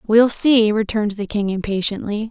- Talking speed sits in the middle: Yes, average, 155 wpm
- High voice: Yes, high, 215 Hz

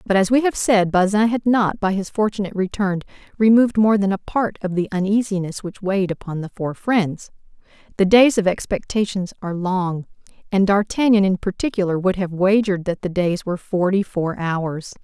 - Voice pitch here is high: Yes, high, 195 Hz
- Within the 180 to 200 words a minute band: Yes, average, 185 wpm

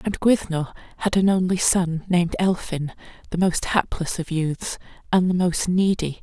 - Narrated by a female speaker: Yes, female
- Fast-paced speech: No, average, 165 wpm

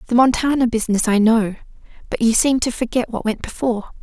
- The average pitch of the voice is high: Yes, high, 235 Hz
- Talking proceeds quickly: No, average, 195 wpm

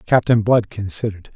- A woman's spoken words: No, male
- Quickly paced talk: No, slow, 135 wpm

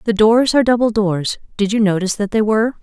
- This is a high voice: Yes, high, 215 Hz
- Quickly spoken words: Yes, fast, 235 wpm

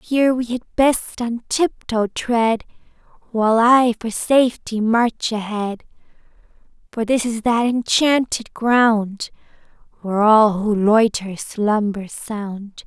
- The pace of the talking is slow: Yes, slow, 120 wpm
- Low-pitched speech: No, high, 225 Hz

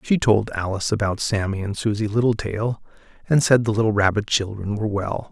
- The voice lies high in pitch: No, low, 105 Hz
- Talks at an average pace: Yes, average, 180 wpm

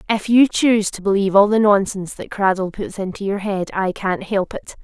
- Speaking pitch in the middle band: No, high, 200 Hz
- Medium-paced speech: No, fast, 225 wpm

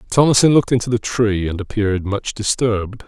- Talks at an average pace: Yes, average, 175 wpm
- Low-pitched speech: Yes, low, 110 Hz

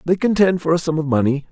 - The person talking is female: No, male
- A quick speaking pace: Yes, fast, 280 wpm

